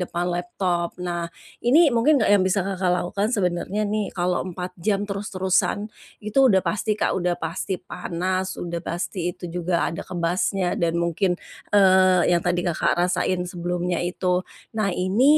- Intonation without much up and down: Yes, narrow, 1.9 semitones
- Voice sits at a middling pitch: Yes, medium, 180 Hz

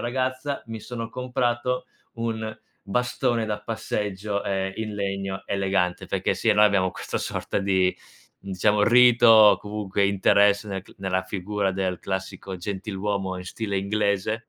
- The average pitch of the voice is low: Yes, low, 105 Hz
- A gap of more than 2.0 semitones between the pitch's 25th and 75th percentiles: Yes, average, 2.7 semitones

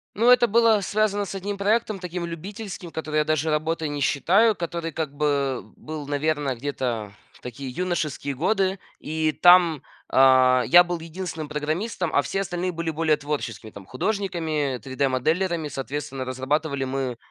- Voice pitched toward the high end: No, medium, 155 Hz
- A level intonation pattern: No, average, 4.5 semitones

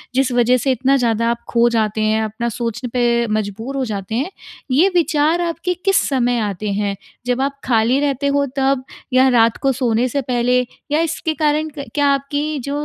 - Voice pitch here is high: Yes, very high, 255 Hz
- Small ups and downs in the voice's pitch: No, average, 3.5 semitones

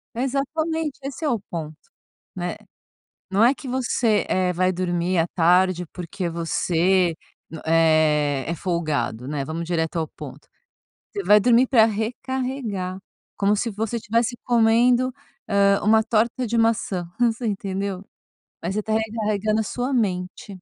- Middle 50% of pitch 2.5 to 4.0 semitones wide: No, average, 5.0 semitones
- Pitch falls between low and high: No, high, 200 Hz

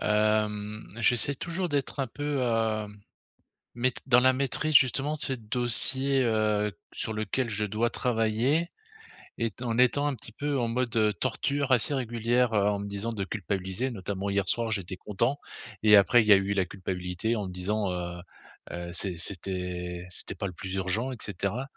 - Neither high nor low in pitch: No, low, 110 Hz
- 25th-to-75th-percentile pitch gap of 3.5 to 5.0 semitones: Yes, average, 4.1 semitones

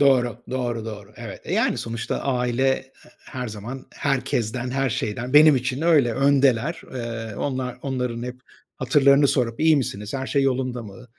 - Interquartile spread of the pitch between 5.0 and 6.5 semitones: No, narrow, 2.5 semitones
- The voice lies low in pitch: Yes, low, 125 Hz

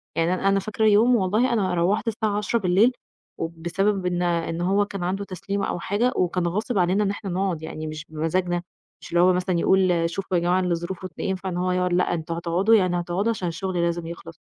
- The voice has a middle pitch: Yes, medium, 180 Hz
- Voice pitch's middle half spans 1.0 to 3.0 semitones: Yes, narrow, 2.5 semitones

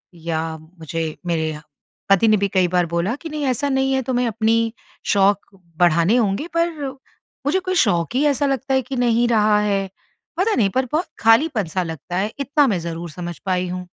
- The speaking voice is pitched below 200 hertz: No, high, 210 Hz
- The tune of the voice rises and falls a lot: Yes, wide, 6.8 semitones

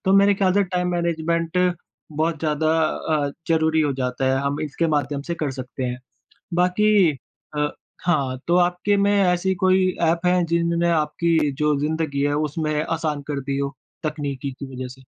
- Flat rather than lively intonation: No, average, 3.6 semitones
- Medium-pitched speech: Yes, medium, 160 Hz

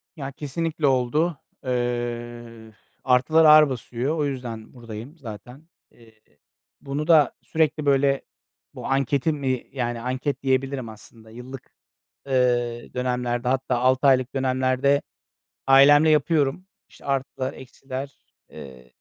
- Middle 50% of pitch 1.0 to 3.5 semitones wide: Yes, narrow, 2.6 semitones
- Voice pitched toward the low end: Yes, low, 130 Hz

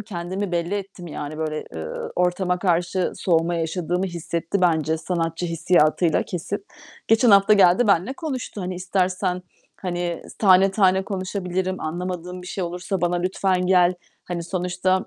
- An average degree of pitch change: No, narrow, 1.7 semitones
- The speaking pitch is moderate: Yes, medium, 180 Hz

